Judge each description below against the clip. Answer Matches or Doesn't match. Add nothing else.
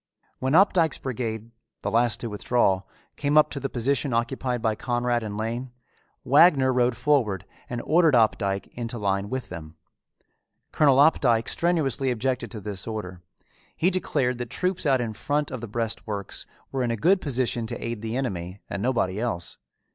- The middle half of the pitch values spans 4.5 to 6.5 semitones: Doesn't match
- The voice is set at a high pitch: Doesn't match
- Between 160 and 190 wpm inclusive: Matches